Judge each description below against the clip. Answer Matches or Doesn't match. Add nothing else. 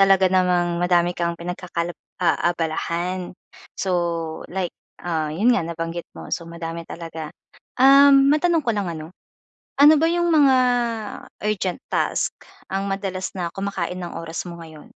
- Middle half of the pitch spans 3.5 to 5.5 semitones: Doesn't match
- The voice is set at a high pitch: Doesn't match